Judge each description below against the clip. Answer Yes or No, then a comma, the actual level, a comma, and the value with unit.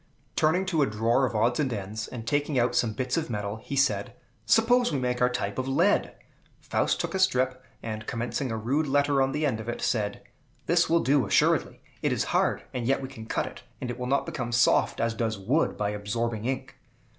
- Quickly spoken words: Yes, fast, 225 wpm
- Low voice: Yes, low, 125 Hz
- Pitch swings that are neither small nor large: Yes, average, 4.0 semitones